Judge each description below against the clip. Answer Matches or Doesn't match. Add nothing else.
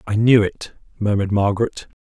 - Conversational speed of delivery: Matches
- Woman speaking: Doesn't match